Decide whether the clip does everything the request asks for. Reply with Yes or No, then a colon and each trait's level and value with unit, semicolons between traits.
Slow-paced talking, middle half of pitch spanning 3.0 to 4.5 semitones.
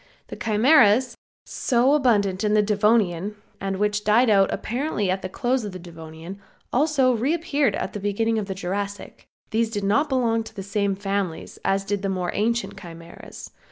No: average, 175 wpm; average, 3.4 semitones